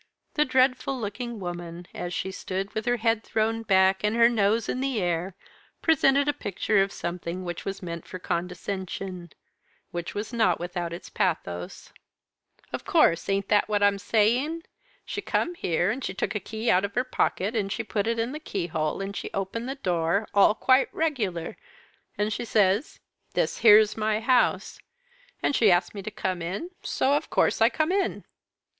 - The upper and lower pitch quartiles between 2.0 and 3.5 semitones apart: No, average, 4.4 semitones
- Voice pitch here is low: No, high, 205 Hz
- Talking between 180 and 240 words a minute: Yes, average, 185 wpm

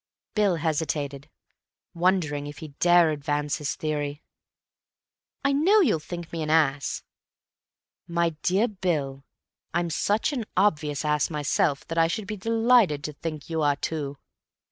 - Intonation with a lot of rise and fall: No, average, 4.1 semitones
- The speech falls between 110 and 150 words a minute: Yes, average, 145 wpm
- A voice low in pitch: No, medium, 160 Hz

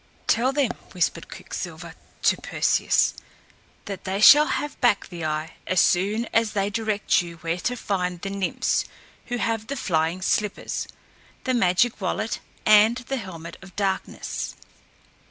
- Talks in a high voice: Yes, high, 200 Hz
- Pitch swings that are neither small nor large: Yes, average, 4.2 semitones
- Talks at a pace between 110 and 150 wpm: Yes, average, 145 wpm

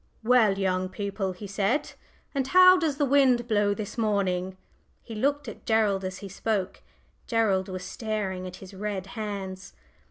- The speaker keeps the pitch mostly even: No, average, 3.4 semitones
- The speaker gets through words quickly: No, average, 160 wpm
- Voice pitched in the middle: No, high, 205 Hz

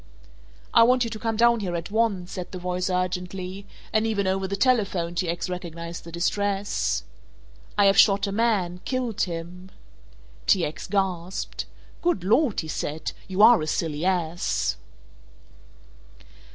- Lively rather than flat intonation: No, average, 3.2 semitones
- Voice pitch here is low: No, high, 190 Hz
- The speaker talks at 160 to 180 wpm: No, average, 150 wpm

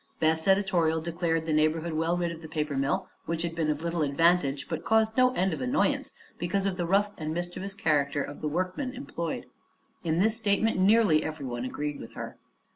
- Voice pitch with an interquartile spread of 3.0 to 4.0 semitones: Yes, average, 3.7 semitones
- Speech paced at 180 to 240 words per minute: Yes, average, 200 wpm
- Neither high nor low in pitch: Yes, medium, 170 Hz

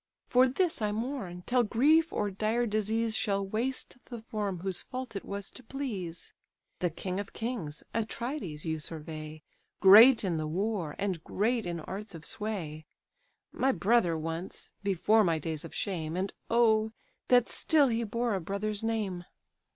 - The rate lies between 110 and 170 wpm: Yes, average, 160 wpm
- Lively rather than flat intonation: No, average, 4.9 semitones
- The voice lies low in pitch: No, high, 205 Hz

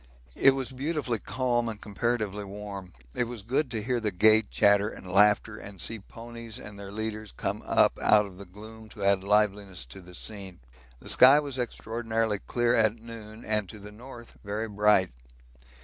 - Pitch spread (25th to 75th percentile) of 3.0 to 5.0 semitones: No, narrow, 2.6 semitones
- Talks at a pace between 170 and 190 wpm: Yes, average, 180 wpm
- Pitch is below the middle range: Yes, low, 110 Hz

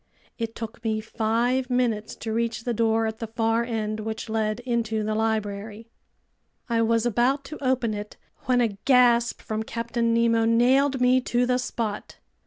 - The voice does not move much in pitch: Yes, narrow, 1.7 semitones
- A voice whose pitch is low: No, high, 230 Hz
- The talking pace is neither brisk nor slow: Yes, average, 170 wpm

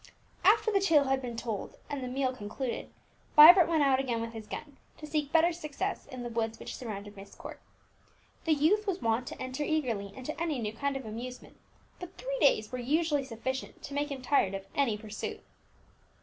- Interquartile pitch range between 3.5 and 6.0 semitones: Yes, average, 5.1 semitones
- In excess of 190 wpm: Yes, fast, 205 wpm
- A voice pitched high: Yes, very high, 265 Hz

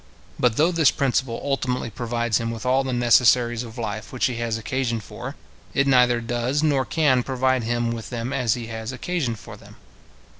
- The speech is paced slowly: No, average, 190 wpm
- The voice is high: No, low, 120 Hz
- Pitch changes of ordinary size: No, narrow, 2.2 semitones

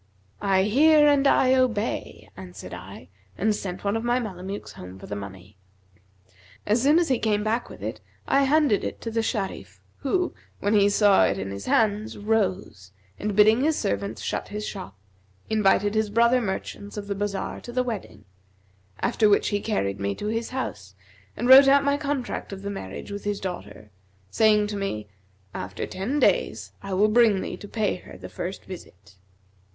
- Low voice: No, high, 205 Hz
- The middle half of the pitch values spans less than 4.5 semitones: Yes, average, 3.9 semitones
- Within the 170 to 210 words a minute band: Yes, average, 180 wpm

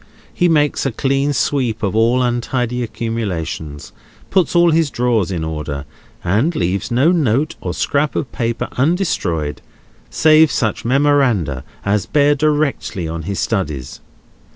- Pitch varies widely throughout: Yes, wide, 7.1 semitones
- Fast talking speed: No, slow, 135 wpm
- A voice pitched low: Yes, low, 120 Hz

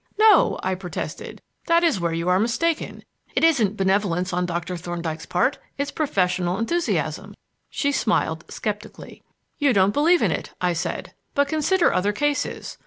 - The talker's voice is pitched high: Yes, high, 205 Hz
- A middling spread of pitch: No, wide, 8.4 semitones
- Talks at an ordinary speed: Yes, average, 155 wpm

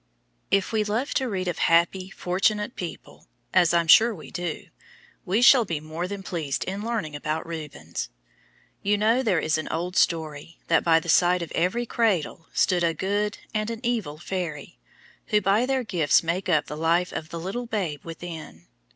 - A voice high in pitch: No, medium, 180 Hz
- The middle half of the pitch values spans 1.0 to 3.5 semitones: No, average, 4.3 semitones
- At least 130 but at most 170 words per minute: No, average, 185 wpm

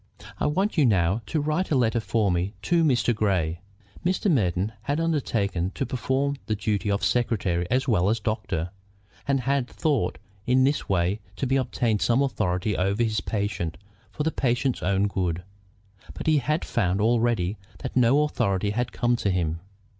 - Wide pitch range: Yes, wide, 5.7 semitones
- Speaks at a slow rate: No, average, 170 wpm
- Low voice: Yes, low, 115 Hz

